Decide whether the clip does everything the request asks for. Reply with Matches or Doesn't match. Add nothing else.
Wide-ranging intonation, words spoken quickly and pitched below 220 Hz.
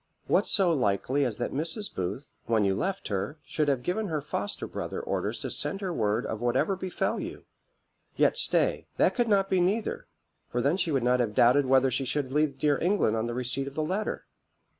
Matches